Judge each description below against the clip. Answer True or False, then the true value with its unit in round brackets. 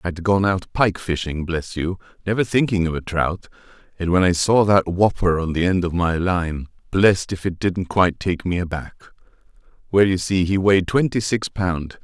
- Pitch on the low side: True (90 Hz)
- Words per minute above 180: True (200 wpm)